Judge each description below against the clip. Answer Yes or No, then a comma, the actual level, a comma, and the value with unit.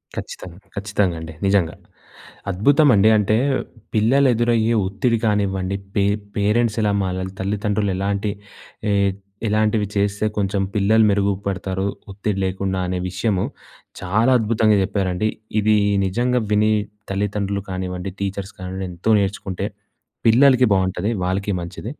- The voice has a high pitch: No, low, 100 Hz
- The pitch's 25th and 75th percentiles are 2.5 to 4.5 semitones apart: No, narrow, 2.1 semitones